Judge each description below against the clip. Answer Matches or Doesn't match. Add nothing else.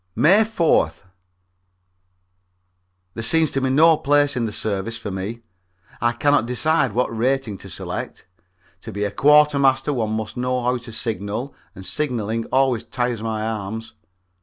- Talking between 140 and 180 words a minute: Matches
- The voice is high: Doesn't match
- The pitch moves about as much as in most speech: Matches